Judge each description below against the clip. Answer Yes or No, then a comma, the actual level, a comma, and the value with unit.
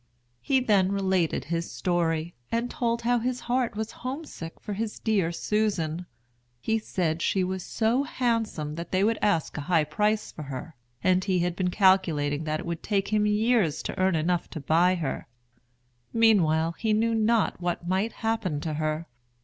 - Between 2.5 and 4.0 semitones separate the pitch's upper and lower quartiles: No, average, 5.1 semitones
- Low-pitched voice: No, medium, 185 Hz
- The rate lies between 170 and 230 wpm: Yes, average, 175 wpm